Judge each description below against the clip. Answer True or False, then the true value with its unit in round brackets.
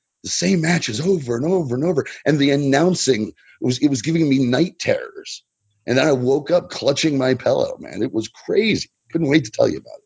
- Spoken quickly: True (220 wpm)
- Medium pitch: True (145 Hz)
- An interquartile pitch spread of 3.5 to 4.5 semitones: False (5.2 semitones)